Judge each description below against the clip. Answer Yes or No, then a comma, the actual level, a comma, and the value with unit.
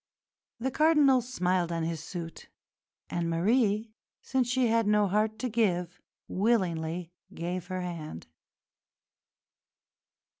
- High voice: Yes, high, 195 Hz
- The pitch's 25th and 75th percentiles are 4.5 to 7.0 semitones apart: Yes, average, 5.2 semitones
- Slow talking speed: Yes, slow, 110 wpm